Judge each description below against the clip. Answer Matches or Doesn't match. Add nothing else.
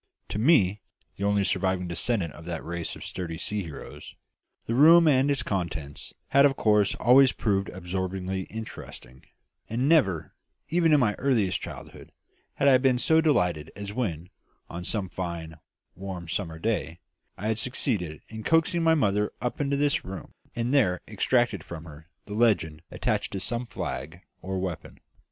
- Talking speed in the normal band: Matches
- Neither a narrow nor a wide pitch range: Doesn't match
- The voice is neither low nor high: Doesn't match